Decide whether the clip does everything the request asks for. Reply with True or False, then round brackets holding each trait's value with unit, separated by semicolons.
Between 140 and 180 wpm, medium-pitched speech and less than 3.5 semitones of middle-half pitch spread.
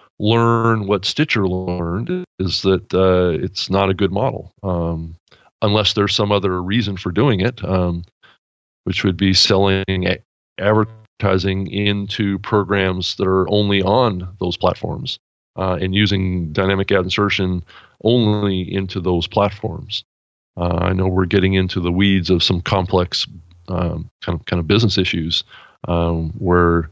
False (145 wpm; 95 Hz; 2.4 semitones)